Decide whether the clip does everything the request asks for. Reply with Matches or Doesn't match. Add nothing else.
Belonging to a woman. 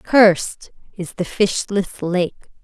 Matches